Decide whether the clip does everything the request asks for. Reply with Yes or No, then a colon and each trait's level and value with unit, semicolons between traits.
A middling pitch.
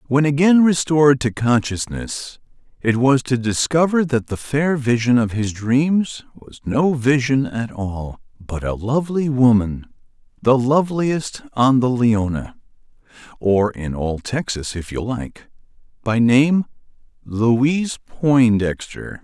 No: low, 125 Hz